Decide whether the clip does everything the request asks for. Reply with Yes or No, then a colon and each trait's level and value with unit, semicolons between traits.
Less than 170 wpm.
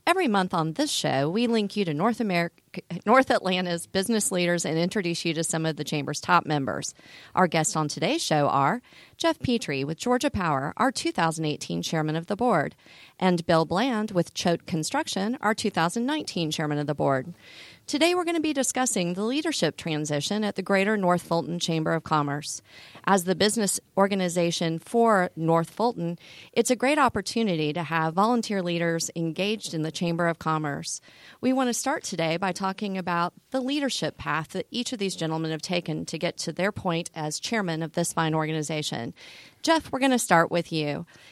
No: average, 185 wpm